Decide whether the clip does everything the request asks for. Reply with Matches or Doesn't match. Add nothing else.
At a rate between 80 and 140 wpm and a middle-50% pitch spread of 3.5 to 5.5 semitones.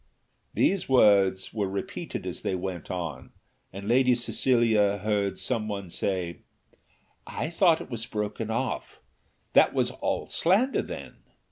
Matches